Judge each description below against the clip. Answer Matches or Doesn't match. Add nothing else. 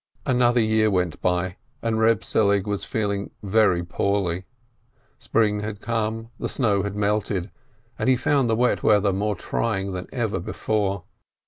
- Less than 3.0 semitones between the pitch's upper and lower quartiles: Matches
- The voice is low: Matches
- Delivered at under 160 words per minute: Matches